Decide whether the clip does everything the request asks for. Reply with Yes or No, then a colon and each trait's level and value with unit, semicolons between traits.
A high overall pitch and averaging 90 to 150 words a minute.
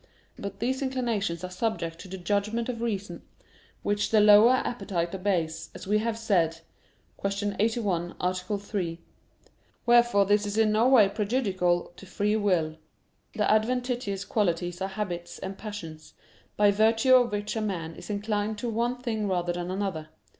No: high, 205 Hz; average, 160 wpm